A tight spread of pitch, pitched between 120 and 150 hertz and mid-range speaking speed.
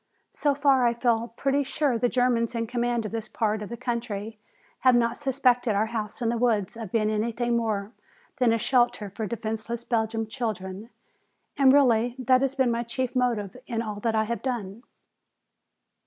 No: narrow, 2.2 semitones; high, 235 Hz; average, 185 wpm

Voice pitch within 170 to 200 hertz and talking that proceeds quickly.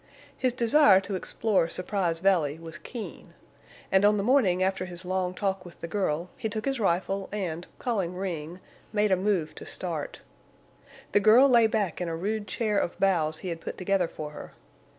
No: high, 190 Hz; average, 190 wpm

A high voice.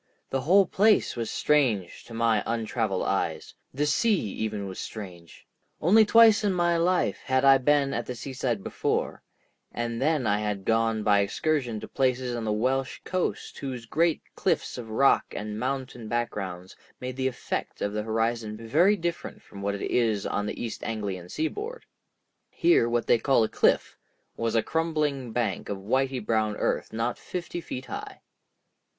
No: low, 120 Hz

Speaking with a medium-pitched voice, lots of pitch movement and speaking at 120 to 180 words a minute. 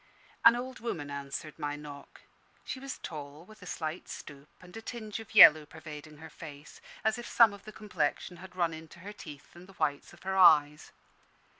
No: medium, 165 Hz; wide, 5.8 semitones; average, 195 wpm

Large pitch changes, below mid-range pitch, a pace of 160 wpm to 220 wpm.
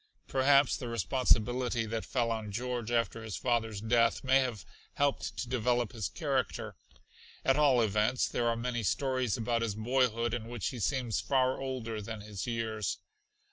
No: narrow, 2.4 semitones; low, 120 Hz; average, 165 wpm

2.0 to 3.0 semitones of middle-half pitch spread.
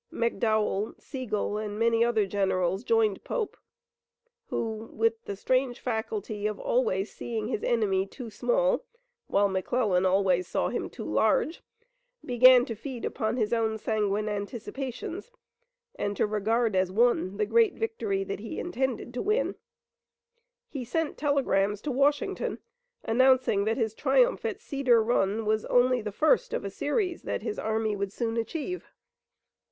No: average, 3.7 semitones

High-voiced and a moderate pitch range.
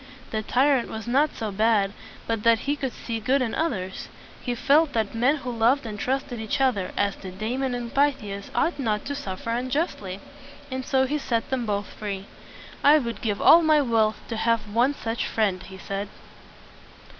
Yes: high, 230 Hz; average, 4.2 semitones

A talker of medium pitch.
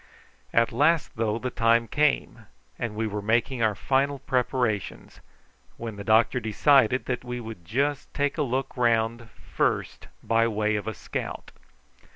No: low, 115 Hz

